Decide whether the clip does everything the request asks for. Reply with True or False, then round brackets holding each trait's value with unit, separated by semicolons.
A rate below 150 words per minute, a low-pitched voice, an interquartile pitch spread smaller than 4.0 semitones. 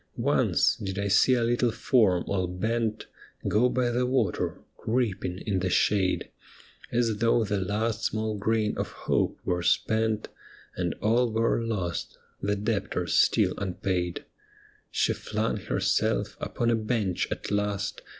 True (140 wpm; 105 Hz; 3.2 semitones)